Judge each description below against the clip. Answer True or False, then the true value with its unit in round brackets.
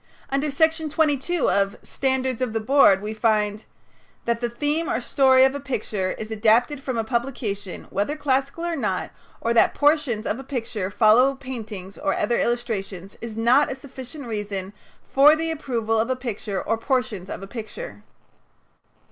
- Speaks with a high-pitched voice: True (240 Hz)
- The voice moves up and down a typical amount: True (4.2 semitones)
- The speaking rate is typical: True (170 wpm)